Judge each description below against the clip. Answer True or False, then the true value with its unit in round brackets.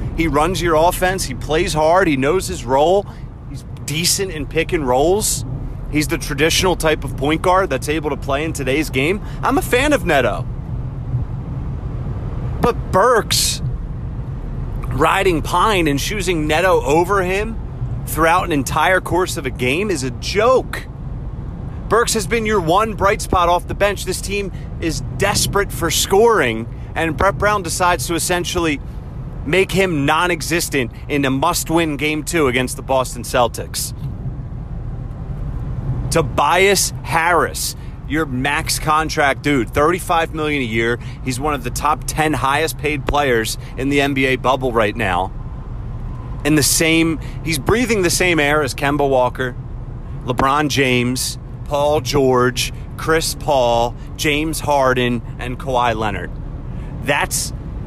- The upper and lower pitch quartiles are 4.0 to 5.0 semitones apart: True (4.3 semitones)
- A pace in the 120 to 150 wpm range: True (140 wpm)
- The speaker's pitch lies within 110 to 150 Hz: True (140 Hz)